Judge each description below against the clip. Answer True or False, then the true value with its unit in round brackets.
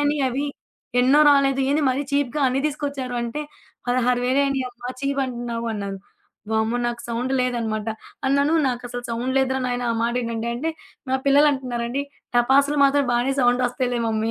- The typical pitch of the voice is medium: False (250 Hz)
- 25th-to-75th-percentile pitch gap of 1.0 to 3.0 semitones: True (2.6 semitones)